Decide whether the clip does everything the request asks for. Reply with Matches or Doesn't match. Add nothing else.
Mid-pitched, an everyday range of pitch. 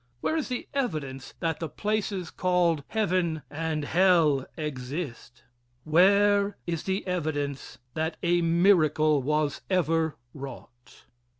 Matches